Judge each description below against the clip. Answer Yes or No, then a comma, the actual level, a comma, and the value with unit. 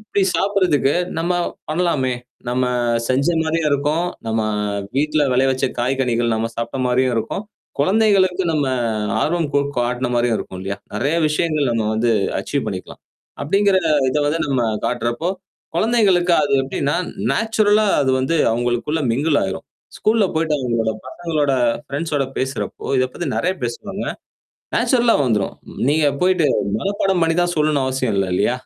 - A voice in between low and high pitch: Yes, medium, 145 Hz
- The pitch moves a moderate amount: No, wide, 5.8 semitones